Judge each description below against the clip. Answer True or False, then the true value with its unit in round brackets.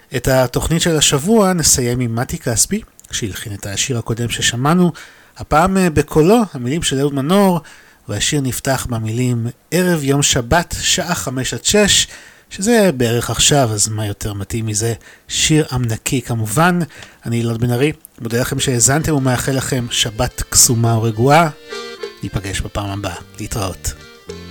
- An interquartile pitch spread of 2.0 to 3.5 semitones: False (4.8 semitones)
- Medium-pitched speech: False (125 Hz)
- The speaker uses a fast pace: False (135 wpm)